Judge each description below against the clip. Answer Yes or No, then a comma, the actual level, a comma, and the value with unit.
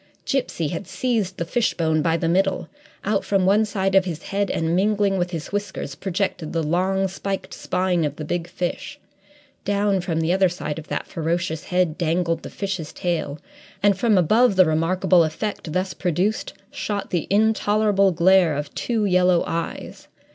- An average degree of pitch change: Yes, average, 3.1 semitones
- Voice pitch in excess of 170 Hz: Yes, medium, 185 Hz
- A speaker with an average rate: Yes, average, 170 wpm